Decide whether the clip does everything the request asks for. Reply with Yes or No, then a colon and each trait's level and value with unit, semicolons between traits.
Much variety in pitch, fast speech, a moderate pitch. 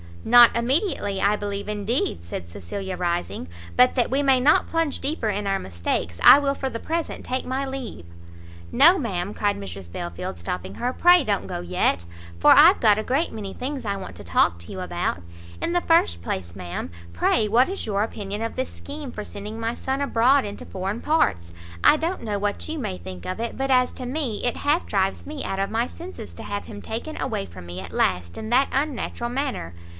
No: wide, 7.0 semitones; fast, 210 wpm; high, 220 Hz